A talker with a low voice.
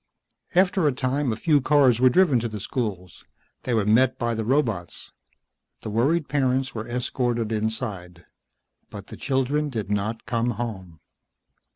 Yes: low, 120 Hz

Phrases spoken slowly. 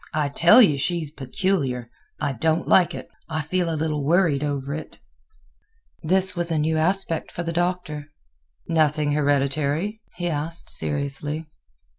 No: average, 145 wpm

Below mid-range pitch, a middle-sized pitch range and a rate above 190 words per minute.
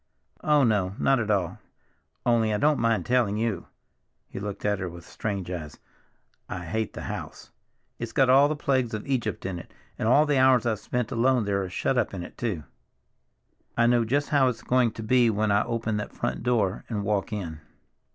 Yes: low, 110 Hz; average, 3.9 semitones; average, 200 wpm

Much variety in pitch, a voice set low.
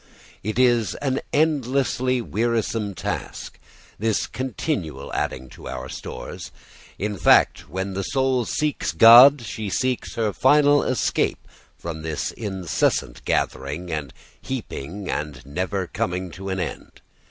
Yes: wide, 6.6 semitones; low, 105 Hz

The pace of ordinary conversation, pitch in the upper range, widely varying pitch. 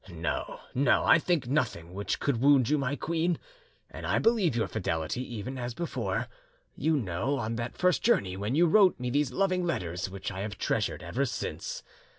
No: average, 185 wpm; low, 125 Hz; wide, 7.9 semitones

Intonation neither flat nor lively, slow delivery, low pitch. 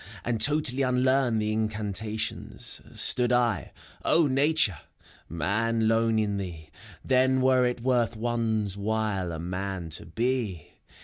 Yes: average, 4.0 semitones; slow, 130 wpm; low, 110 Hz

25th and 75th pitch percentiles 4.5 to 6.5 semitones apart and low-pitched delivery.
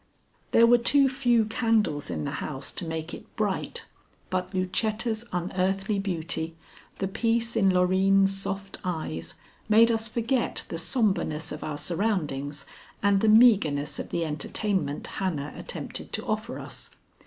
No: wide, 5.6 semitones; high, 195 Hz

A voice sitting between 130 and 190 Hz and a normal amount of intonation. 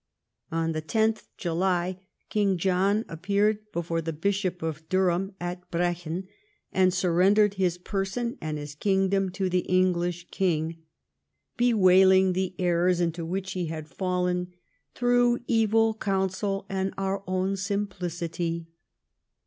No: medium, 185 Hz; narrow, 2.1 semitones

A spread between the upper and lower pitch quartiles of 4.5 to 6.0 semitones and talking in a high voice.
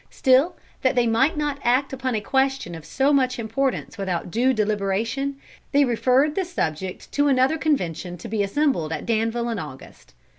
Yes: average, 5.2 semitones; high, 245 Hz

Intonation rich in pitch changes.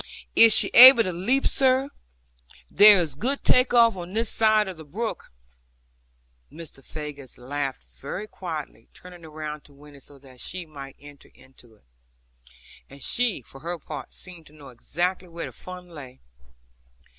Yes: wide, 6.6 semitones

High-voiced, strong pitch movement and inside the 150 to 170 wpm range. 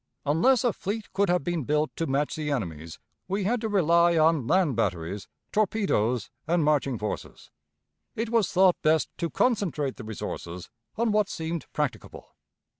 No: medium, 165 Hz; wide, 6.6 semitones; average, 160 wpm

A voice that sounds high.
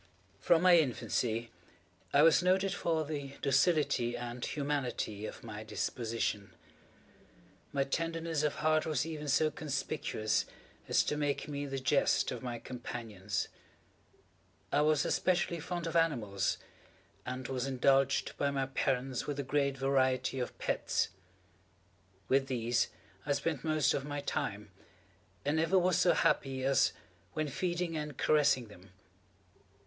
No: medium, 140 Hz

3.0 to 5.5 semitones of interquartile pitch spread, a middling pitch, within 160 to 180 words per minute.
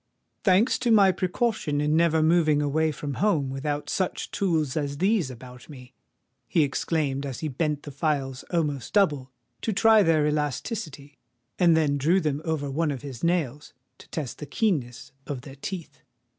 Yes: average, 3.6 semitones; medium, 150 Hz; average, 170 wpm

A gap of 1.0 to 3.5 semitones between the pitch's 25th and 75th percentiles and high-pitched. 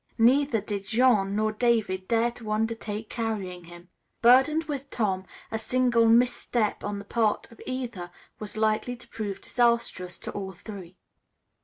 Yes: average, 3.1 semitones; high, 220 Hz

